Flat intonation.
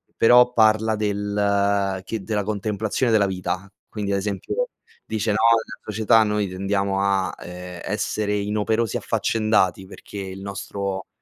Yes: narrow, 1.8 semitones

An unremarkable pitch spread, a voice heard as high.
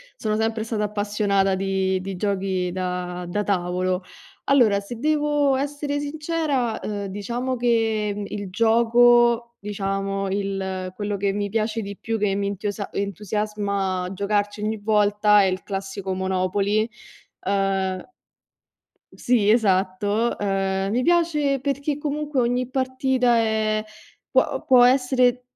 Yes: average, 3.7 semitones; high, 210 Hz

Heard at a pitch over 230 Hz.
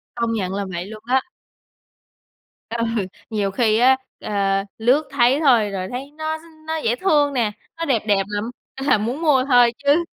Yes: high, 240 Hz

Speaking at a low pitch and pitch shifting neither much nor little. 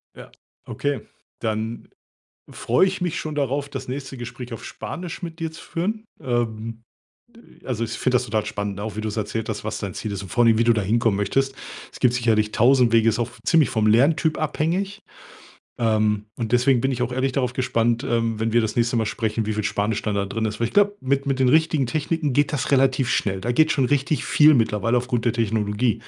Yes: low, 120 Hz; average, 3.8 semitones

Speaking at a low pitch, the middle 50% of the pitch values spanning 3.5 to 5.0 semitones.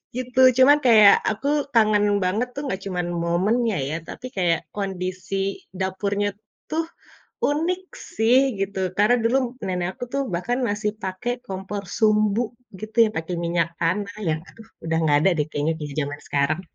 No: high, 200 Hz; average, 4.2 semitones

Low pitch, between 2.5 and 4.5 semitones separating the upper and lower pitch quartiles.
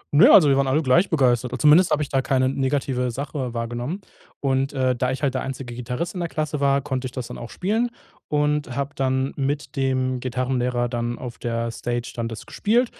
Yes: low, 130 Hz; average, 2.9 semitones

